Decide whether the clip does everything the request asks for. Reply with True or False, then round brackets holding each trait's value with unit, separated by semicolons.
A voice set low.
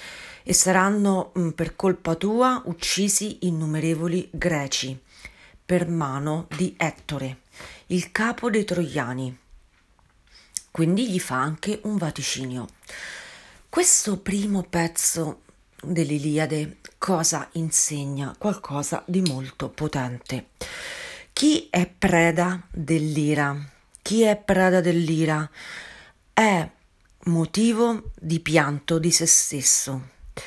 False (165 Hz)